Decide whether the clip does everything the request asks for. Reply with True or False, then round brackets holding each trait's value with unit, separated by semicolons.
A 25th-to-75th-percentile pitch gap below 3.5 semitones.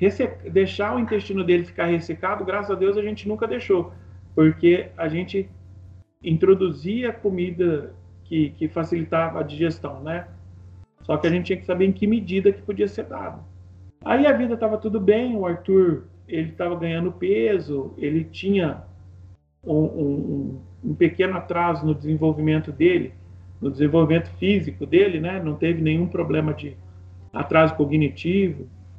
False (5.2 semitones)